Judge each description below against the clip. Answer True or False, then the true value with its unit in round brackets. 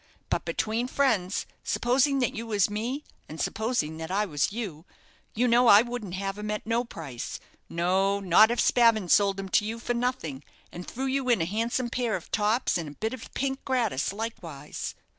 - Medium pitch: False (220 Hz)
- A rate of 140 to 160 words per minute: False (195 wpm)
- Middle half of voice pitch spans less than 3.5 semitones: False (4.4 semitones)